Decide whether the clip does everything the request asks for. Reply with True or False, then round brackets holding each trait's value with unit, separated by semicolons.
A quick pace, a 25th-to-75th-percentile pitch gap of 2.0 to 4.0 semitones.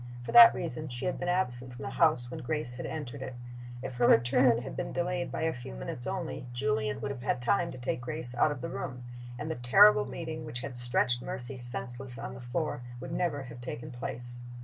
False (225 wpm; 4.4 semitones)